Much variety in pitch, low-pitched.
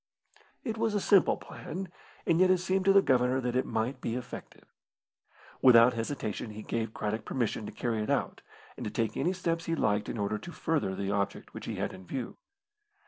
Yes: wide, 7.7 semitones; low, 125 Hz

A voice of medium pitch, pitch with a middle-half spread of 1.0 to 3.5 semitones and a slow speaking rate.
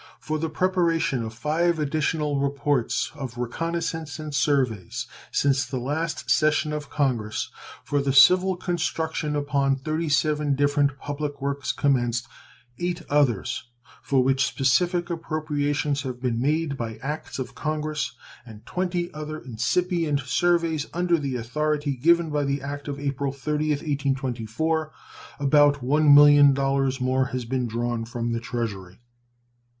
Yes: medium, 145 Hz; average, 2.9 semitones; slow, 130 wpm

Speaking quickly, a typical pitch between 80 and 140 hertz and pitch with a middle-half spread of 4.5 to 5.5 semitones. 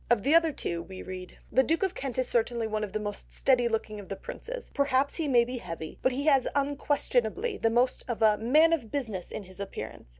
No: fast, 235 wpm; high, 245 Hz; average, 5.0 semitones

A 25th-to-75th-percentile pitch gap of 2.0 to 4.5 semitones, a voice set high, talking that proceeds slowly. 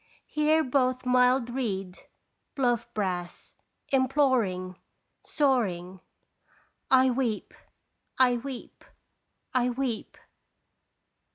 Yes: average, 4.1 semitones; very high, 250 Hz; slow, 75 wpm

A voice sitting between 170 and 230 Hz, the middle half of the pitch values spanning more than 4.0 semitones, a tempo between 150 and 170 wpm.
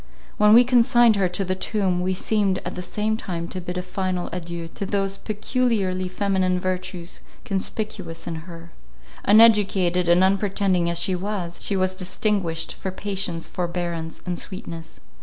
No: medium, 185 Hz; narrow, 2.5 semitones; average, 160 wpm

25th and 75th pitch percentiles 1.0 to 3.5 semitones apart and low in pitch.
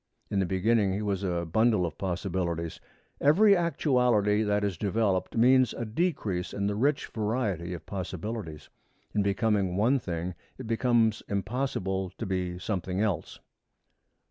No: average, 4.0 semitones; low, 100 Hz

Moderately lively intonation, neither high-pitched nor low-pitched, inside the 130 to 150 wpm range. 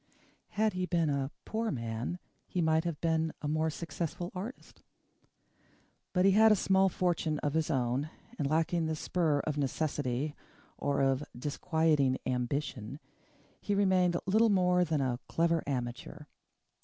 Yes: average, 4.3 semitones; medium, 160 Hz; average, 145 wpm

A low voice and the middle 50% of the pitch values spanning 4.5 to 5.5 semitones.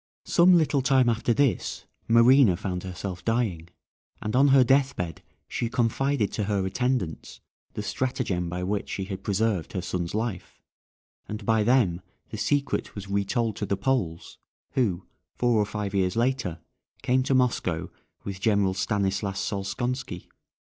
Yes: low, 105 Hz; average, 4.9 semitones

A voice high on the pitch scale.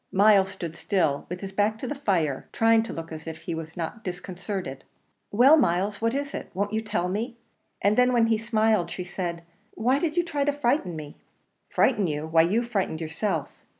Yes: high, 200 Hz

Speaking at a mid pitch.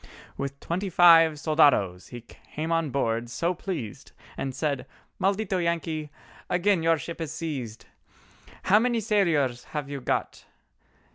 Yes: medium, 160 Hz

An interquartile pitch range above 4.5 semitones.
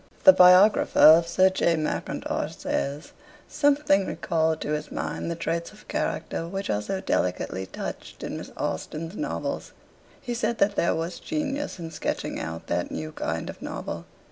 Yes: average, 4.9 semitones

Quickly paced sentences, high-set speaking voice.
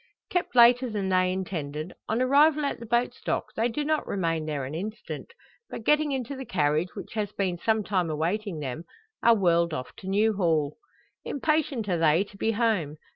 No: average, 190 wpm; high, 200 Hz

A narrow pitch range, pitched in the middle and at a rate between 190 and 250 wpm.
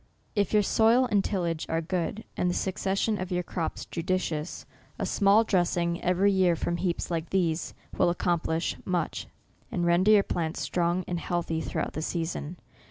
No: narrow, 2.3 semitones; medium, 175 Hz; average, 165 wpm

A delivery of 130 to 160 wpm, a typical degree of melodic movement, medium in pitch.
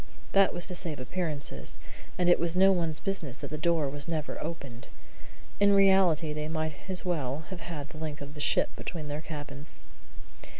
No: average, 185 wpm; average, 3.1 semitones; medium, 160 Hz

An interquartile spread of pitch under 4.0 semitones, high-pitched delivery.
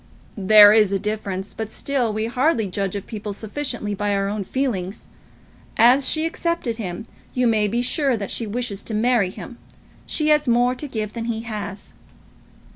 Yes: average, 3.4 semitones; high, 220 Hz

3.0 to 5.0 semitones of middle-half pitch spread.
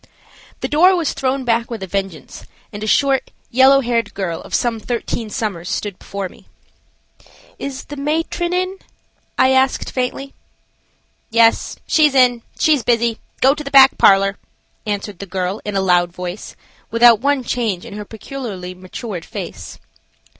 No: wide, 5.4 semitones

